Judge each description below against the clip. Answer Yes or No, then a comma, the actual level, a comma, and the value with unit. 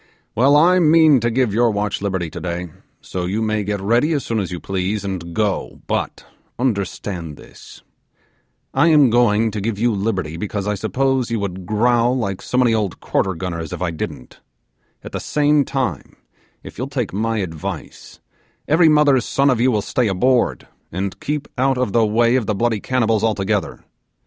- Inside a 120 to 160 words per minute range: No, average, 185 wpm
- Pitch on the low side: Yes, low, 110 Hz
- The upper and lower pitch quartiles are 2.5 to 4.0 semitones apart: No, average, 4.7 semitones